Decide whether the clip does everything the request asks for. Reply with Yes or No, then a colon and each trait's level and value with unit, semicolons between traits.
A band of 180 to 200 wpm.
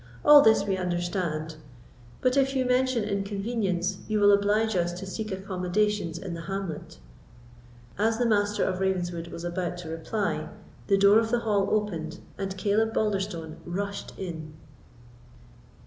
No: average, 145 wpm